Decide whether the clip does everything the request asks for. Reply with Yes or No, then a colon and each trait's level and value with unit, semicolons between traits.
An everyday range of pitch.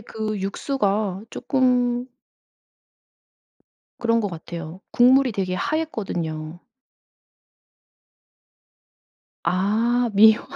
Yes: average, 4.9 semitones